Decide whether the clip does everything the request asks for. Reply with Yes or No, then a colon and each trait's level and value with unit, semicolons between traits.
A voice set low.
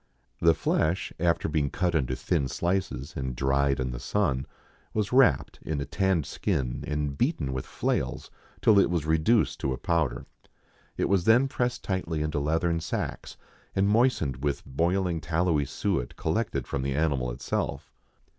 Yes: very low, 80 Hz